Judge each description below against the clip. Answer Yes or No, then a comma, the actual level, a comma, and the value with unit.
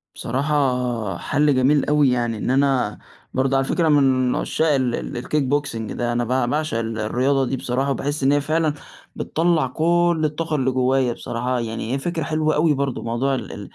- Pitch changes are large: No, average, 3.2 semitones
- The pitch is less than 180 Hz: Yes, low, 135 Hz